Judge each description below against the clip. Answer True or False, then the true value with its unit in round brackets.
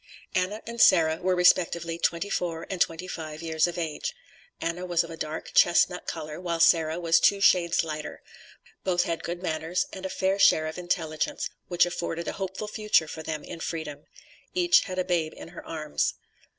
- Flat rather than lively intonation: True (2.2 semitones)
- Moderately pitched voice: True (170 Hz)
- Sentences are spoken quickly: False (190 wpm)